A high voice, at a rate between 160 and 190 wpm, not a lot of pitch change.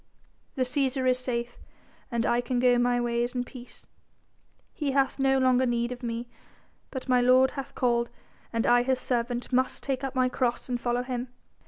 Yes: very high, 250 Hz; average, 185 wpm; narrow, 1.2 semitones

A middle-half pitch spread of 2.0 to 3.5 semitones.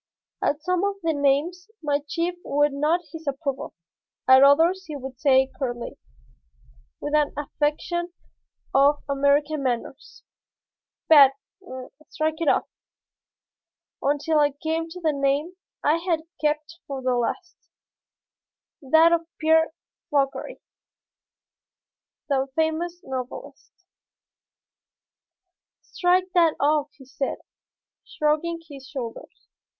Yes: average, 3.0 semitones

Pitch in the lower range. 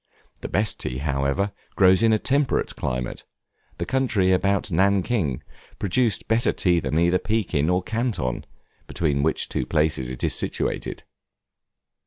Yes: very low, 90 Hz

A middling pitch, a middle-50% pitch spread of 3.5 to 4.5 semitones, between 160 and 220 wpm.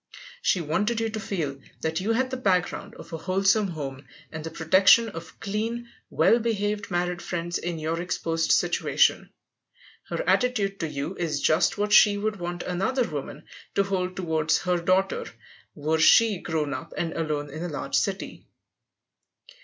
Yes: medium, 180 Hz; average, 4.2 semitones; average, 165 wpm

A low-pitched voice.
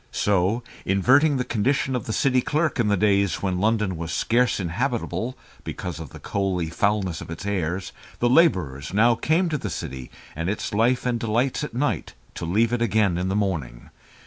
Yes: low, 105 Hz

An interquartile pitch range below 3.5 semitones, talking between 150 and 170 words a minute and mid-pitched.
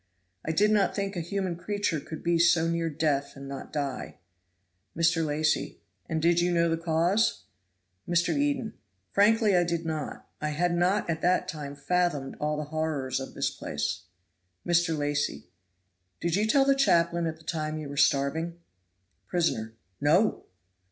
Yes: average, 2.8 semitones; average, 165 wpm; medium, 165 Hz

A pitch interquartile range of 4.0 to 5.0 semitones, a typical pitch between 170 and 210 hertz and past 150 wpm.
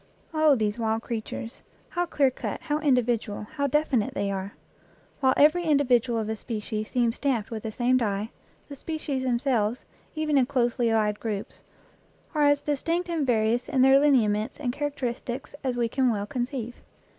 No: average, 4.3 semitones; high, 245 Hz; average, 170 wpm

